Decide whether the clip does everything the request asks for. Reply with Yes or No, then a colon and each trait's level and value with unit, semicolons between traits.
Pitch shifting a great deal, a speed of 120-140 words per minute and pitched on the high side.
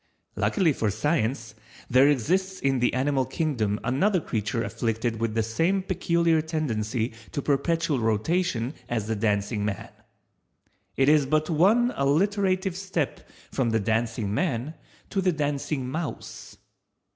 No: wide, 6.8 semitones; slow, 135 wpm; low, 135 Hz